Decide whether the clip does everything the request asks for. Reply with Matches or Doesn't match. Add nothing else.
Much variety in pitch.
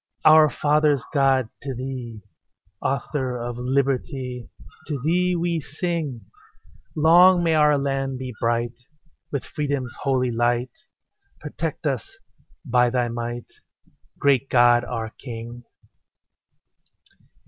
Doesn't match